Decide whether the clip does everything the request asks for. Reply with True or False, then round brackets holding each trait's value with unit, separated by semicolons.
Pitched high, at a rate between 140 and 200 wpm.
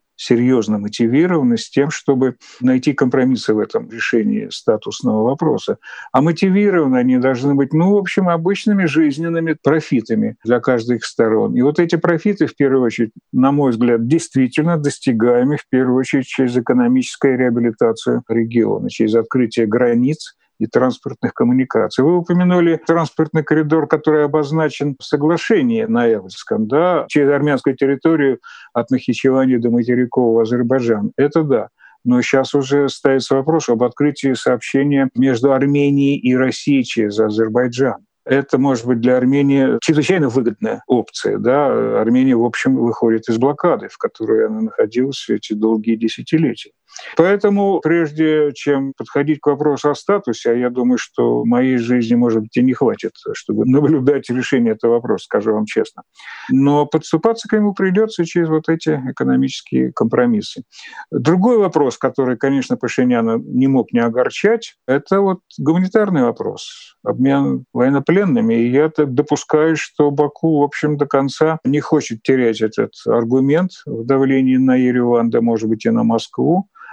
False (140 Hz; 145 wpm)